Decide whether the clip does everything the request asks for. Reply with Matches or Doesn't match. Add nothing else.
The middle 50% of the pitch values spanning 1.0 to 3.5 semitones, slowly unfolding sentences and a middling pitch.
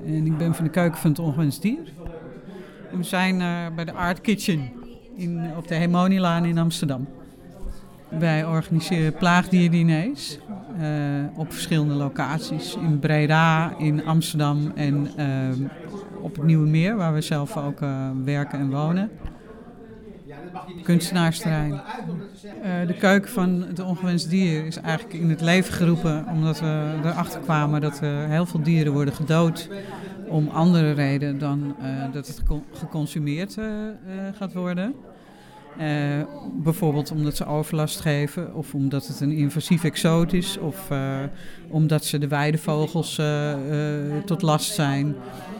Matches